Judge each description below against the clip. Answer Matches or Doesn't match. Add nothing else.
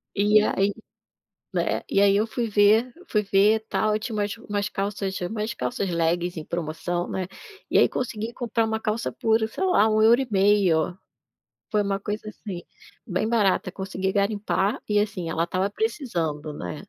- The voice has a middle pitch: Doesn't match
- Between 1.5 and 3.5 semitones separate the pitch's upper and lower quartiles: Matches